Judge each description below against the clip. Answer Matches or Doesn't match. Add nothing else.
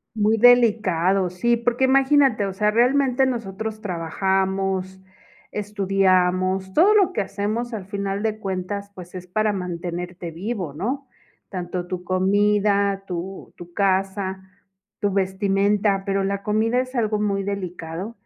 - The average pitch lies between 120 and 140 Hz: Doesn't match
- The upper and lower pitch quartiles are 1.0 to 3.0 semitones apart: Matches